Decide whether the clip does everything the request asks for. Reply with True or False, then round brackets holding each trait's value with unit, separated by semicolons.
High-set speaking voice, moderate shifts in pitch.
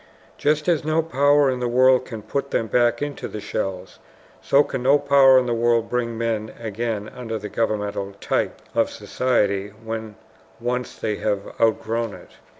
False (115 Hz; 3.3 semitones)